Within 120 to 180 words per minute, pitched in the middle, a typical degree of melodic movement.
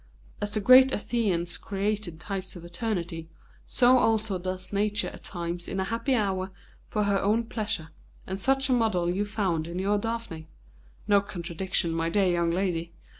No: average, 170 wpm; high, 195 Hz; average, 3.8 semitones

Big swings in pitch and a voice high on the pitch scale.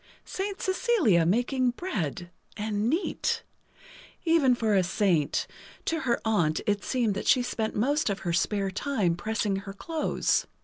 Yes: wide, 5.8 semitones; high, 220 Hz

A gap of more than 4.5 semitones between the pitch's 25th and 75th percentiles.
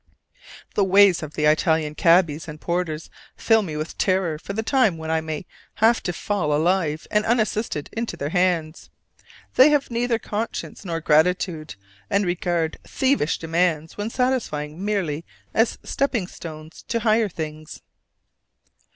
Yes: average, 5.3 semitones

